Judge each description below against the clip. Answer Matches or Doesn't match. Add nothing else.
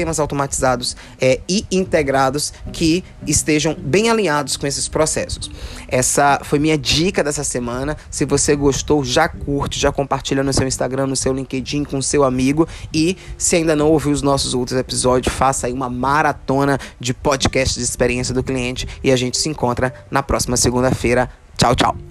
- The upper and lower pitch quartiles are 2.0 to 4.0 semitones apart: Matches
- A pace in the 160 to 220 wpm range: Matches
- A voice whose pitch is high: Doesn't match